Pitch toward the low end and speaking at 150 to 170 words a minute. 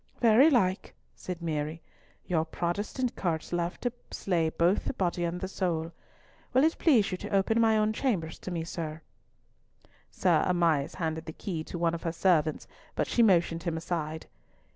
No: medium, 175 Hz; average, 165 wpm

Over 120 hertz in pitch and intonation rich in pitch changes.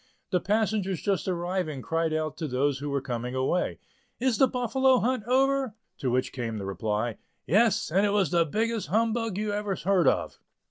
Yes: medium, 185 Hz; wide, 7.7 semitones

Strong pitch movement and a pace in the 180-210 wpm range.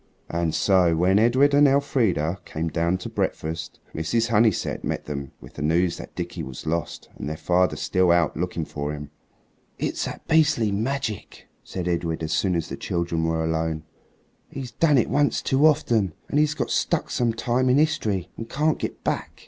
Yes: wide, 7.1 semitones; average, 185 wpm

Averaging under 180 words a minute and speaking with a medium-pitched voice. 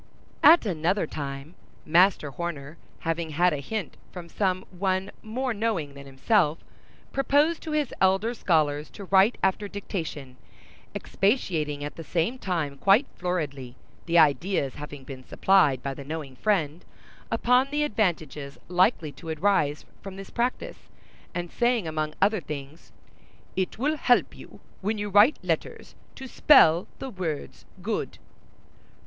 Yes: average, 140 wpm; medium, 180 Hz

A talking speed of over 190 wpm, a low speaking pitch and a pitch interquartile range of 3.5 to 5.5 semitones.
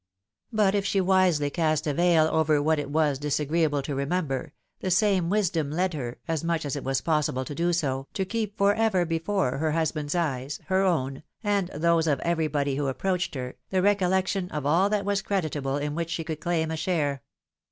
No: fast, 205 wpm; medium, 160 Hz; average, 4.2 semitones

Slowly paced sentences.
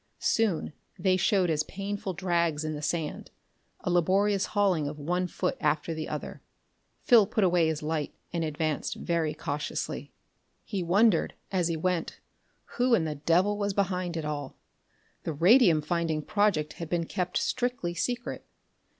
No: average, 155 wpm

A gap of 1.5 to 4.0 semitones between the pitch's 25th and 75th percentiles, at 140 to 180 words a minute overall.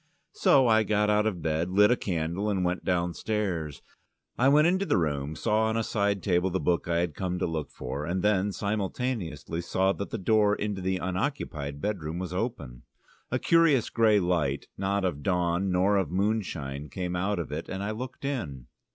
No: average, 3.7 semitones; average, 195 wpm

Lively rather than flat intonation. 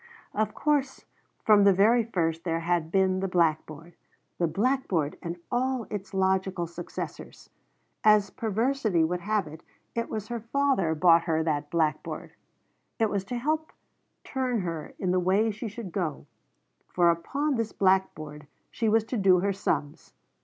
No: average, 5.0 semitones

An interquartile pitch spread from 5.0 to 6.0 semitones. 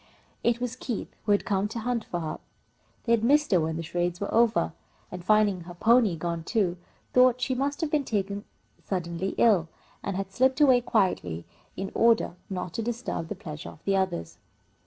Yes: average, 5.3 semitones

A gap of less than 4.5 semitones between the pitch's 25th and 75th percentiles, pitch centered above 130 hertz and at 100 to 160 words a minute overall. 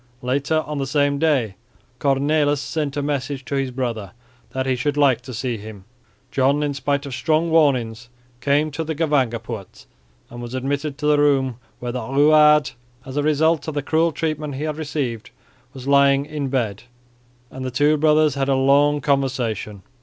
No: narrow, 2.6 semitones; medium, 140 Hz; average, 180 wpm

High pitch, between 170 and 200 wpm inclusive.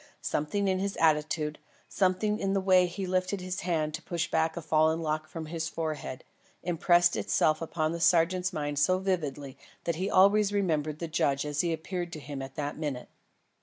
No: medium, 165 Hz; average, 190 wpm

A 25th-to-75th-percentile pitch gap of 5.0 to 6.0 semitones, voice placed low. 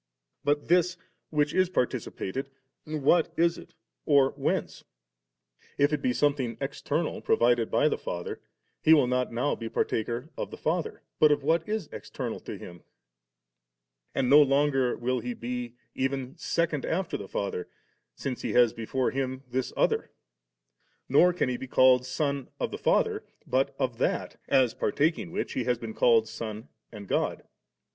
No: average, 3.6 semitones; low, 130 Hz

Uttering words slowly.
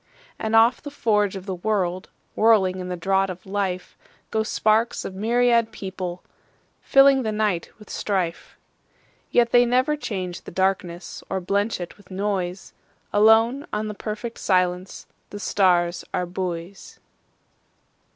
Yes: slow, 120 wpm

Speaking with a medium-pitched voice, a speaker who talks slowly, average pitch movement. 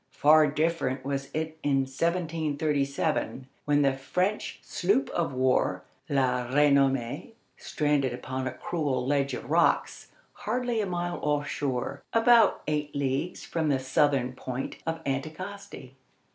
Yes: medium, 145 Hz; slow, 130 wpm; average, 3.5 semitones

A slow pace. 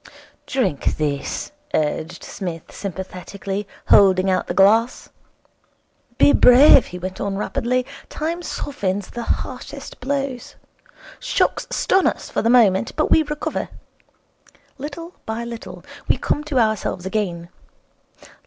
Yes: slow, 120 wpm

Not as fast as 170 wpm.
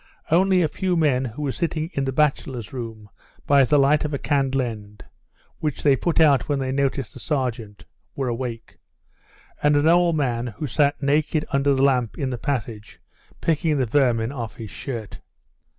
No: average, 180 wpm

